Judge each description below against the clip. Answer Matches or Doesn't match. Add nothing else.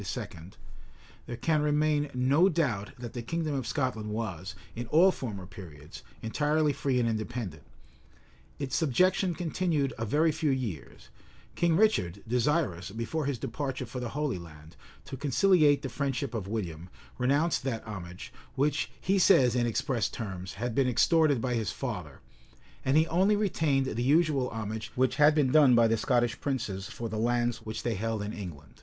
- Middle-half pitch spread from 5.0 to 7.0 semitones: Matches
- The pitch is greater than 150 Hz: Doesn't match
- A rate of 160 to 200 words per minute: Matches